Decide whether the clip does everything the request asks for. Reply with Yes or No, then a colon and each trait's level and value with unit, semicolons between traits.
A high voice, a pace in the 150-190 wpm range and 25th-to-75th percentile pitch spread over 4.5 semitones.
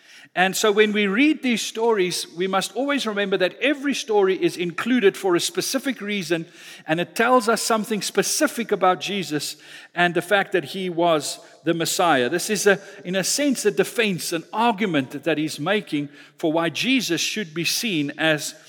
Yes: high, 195 Hz; average, 180 wpm; wide, 5.6 semitones